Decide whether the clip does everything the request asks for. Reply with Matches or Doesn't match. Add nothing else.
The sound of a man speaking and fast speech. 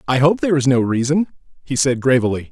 Matches